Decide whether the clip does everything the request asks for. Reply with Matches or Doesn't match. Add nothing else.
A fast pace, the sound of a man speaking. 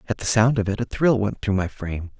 Matches